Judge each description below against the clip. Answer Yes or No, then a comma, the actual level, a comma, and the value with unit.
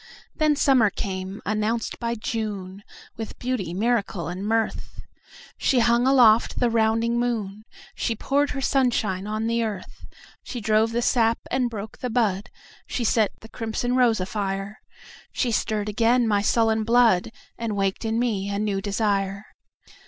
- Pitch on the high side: Yes, high, 220 Hz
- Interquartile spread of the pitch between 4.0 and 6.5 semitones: No, average, 2.8 semitones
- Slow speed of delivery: Yes, slow, 130 wpm